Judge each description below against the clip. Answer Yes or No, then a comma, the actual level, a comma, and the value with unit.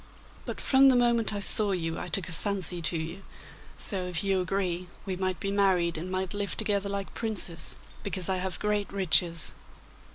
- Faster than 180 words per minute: Yes, average, 190 wpm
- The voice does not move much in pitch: Yes, narrow, 2.3 semitones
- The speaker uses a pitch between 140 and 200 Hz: Yes, high, 190 Hz